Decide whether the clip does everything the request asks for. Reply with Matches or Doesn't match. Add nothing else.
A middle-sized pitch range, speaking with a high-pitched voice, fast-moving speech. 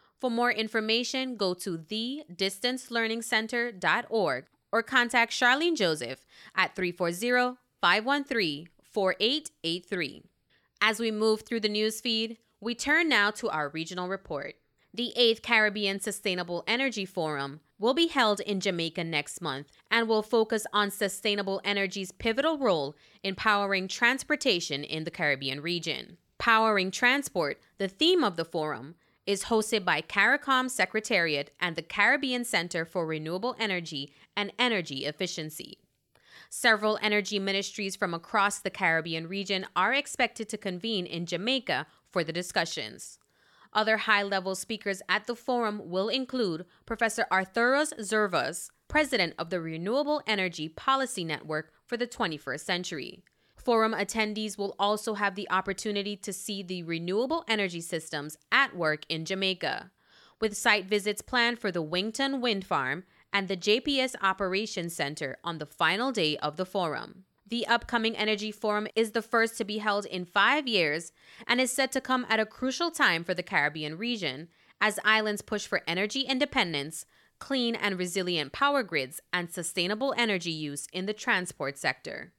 Doesn't match